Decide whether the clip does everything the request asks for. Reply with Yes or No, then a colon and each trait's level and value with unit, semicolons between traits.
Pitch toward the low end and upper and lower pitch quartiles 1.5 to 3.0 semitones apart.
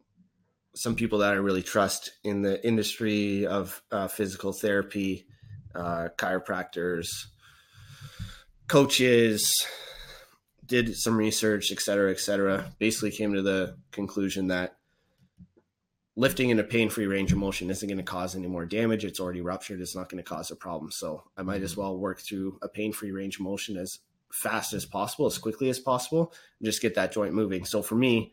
Yes: low, 100 Hz; narrow, 2.4 semitones